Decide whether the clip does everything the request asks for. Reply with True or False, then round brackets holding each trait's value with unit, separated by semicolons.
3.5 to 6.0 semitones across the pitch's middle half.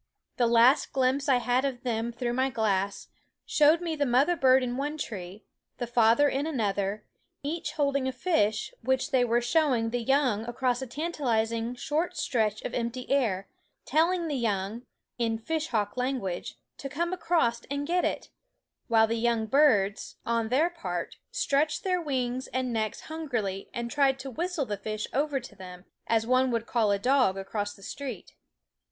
True (4.0 semitones)